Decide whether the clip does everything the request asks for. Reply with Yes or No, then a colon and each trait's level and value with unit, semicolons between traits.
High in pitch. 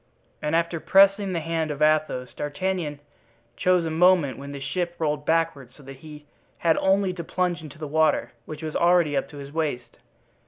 No: medium, 155 Hz